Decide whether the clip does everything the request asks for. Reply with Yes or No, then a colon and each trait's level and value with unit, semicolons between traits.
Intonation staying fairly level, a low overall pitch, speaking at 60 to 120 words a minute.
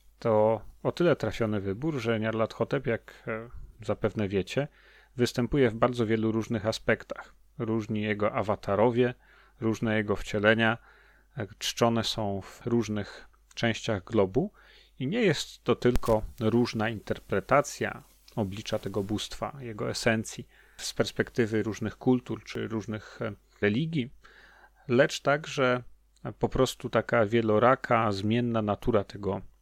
Yes: narrow, 2.3 semitones; low, 110 Hz; average, 115 wpm